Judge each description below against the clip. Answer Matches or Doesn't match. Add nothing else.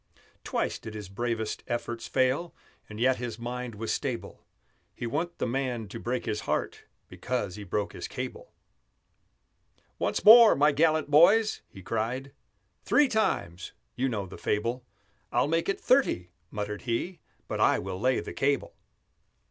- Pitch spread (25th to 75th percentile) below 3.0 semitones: Doesn't match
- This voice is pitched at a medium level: Doesn't match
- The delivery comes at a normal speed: Matches